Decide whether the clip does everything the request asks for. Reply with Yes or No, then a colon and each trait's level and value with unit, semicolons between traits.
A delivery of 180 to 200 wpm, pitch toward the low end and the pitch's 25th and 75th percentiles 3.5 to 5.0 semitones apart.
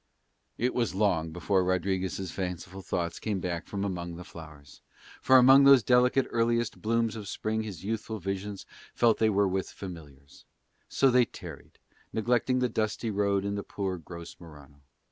No: average, 160 wpm; low, 100 Hz; average, 4.2 semitones